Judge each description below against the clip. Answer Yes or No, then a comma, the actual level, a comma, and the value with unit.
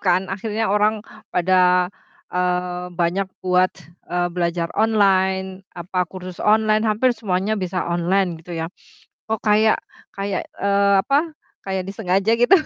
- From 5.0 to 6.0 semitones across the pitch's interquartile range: No, average, 2.8 semitones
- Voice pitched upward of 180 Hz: Yes, high, 190 Hz